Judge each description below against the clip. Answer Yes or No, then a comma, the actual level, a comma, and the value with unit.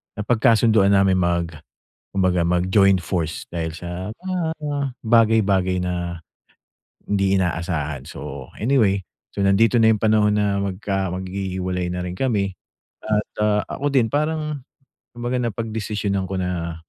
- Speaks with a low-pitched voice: Yes, very low, 95 Hz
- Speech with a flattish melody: No, average, 3.5 semitones